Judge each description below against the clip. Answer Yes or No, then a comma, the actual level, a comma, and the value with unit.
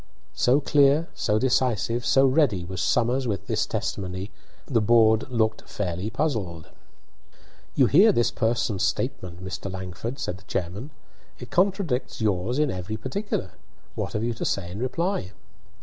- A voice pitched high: No, low, 115 Hz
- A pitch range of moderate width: No, wide, 5.7 semitones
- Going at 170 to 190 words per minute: No, average, 150 wpm